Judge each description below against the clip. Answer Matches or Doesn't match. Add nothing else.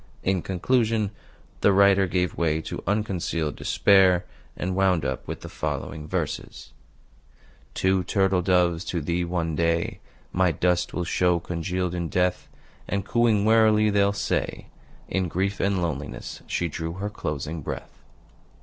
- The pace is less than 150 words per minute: Matches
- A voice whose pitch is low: Matches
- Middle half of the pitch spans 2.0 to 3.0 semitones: Matches